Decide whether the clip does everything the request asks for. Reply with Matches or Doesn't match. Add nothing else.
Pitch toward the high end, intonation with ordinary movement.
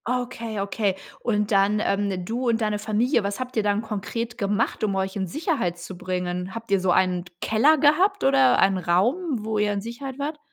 Matches